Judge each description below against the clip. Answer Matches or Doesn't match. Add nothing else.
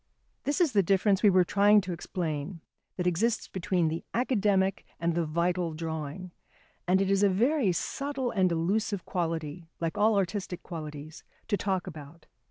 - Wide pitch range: Doesn't match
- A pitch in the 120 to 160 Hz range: Doesn't match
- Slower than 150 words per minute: Doesn't match